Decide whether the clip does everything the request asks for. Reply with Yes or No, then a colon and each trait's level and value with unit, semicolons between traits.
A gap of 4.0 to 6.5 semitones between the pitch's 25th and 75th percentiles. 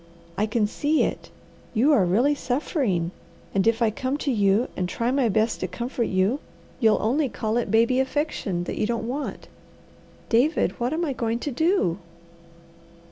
Yes: average, 4.4 semitones